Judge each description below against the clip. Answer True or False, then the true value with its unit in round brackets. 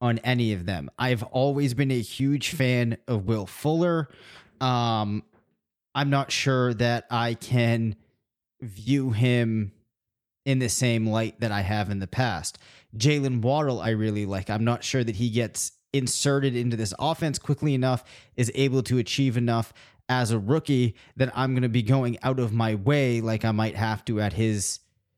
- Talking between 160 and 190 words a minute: True (175 wpm)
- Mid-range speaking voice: False (120 Hz)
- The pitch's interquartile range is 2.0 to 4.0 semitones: True (2.9 semitones)